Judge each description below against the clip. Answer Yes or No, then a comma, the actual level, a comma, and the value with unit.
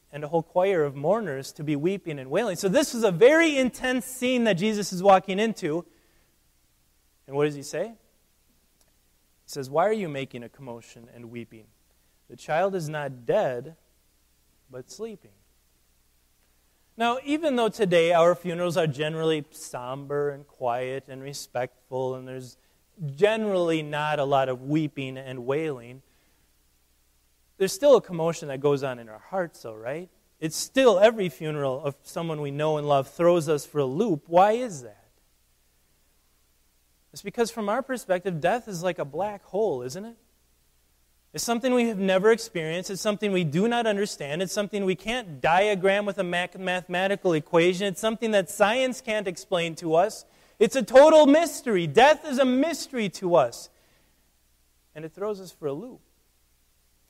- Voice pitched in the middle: Yes, medium, 160 Hz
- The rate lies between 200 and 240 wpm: No, average, 165 wpm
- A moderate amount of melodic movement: No, wide, 8.8 semitones